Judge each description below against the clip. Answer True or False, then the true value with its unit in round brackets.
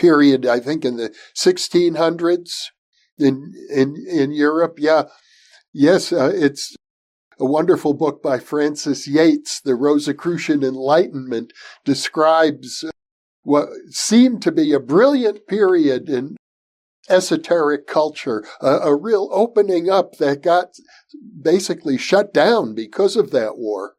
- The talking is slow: True (120 wpm)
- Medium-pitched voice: True (160 Hz)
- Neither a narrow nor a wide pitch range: False (5.7 semitones)